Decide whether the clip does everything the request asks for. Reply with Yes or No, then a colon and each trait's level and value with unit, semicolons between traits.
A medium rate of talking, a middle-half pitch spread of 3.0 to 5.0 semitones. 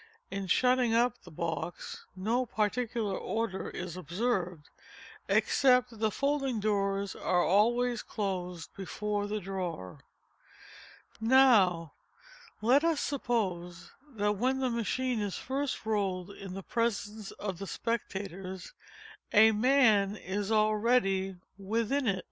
No: slow, 120 wpm; average, 4.0 semitones